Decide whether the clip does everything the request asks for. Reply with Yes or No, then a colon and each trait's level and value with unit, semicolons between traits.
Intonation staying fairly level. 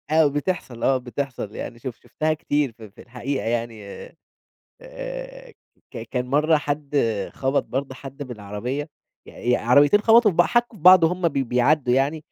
No: average, 4.7 semitones